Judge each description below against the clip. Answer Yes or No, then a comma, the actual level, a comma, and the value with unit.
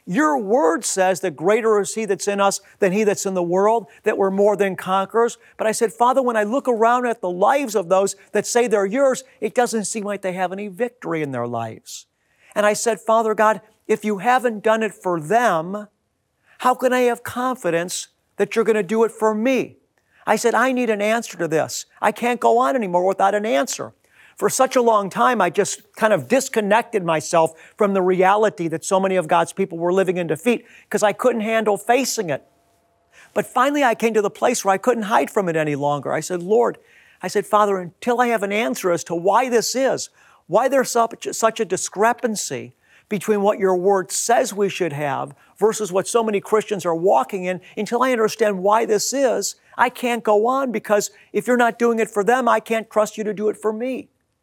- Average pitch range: Yes, average, 3.3 semitones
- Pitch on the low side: No, high, 215 Hz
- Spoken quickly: Yes, fast, 220 wpm